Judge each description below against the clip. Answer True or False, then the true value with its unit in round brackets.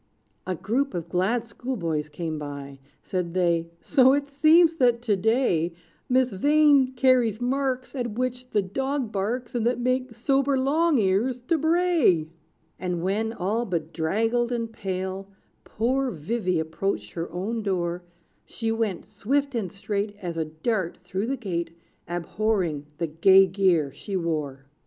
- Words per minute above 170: False (145 wpm)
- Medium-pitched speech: False (215 Hz)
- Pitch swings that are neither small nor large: False (6.4 semitones)